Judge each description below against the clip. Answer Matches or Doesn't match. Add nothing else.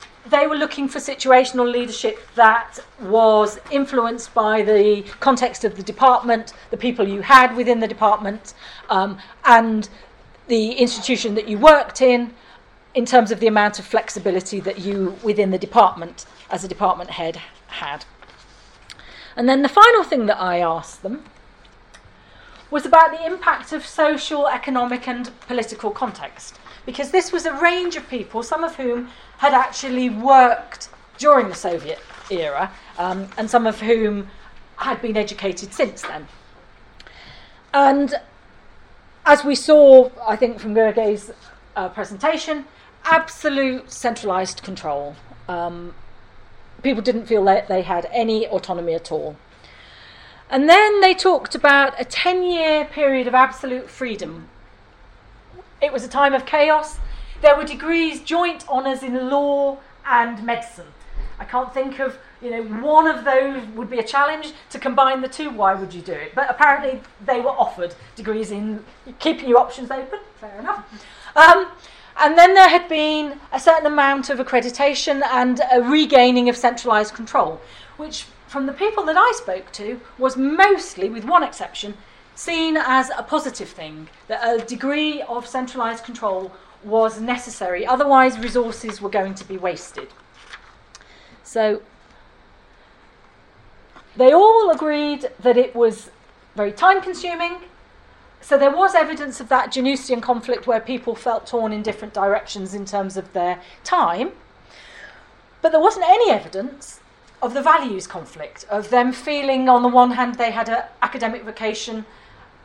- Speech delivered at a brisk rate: Doesn't match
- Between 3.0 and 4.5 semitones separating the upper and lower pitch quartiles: Doesn't match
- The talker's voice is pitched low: Doesn't match